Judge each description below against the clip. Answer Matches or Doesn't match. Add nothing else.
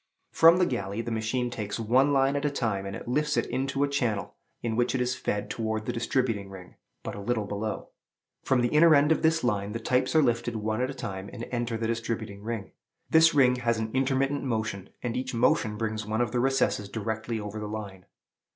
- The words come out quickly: Matches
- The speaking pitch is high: Doesn't match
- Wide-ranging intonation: Doesn't match